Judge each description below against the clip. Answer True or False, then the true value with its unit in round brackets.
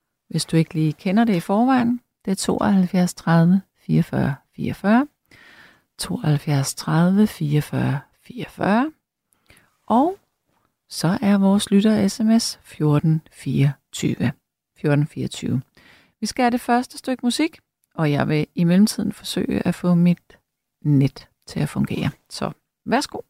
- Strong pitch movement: True (6.3 semitones)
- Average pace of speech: False (130 wpm)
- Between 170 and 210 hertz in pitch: True (185 Hz)